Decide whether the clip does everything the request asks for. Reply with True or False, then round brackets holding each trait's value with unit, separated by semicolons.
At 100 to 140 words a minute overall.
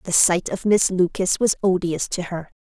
False (205 wpm)